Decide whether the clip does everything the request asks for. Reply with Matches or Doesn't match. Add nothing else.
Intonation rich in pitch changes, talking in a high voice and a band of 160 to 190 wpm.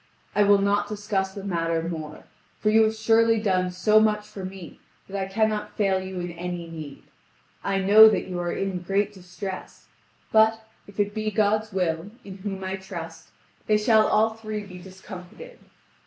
Doesn't match